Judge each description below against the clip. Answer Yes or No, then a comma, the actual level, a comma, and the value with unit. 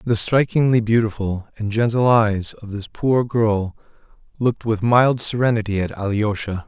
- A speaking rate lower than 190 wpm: Yes, average, 145 wpm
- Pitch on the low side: Yes, low, 110 Hz